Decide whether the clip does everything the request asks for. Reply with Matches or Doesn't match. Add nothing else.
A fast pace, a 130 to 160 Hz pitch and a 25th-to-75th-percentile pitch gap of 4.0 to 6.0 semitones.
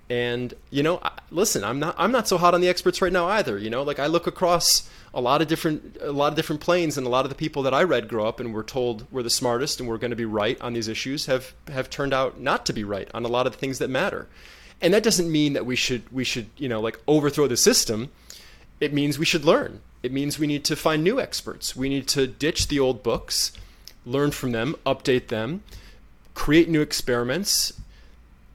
Matches